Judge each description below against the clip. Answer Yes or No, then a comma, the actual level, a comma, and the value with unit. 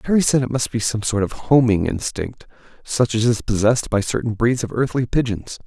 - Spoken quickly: Yes, fast, 210 wpm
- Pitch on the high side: No, low, 115 Hz